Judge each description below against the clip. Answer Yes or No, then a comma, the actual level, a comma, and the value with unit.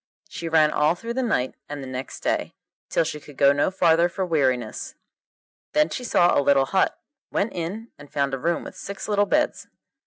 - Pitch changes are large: Yes, wide, 5.9 semitones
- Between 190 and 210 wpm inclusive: Yes, fast, 205 wpm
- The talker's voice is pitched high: No, medium, 165 Hz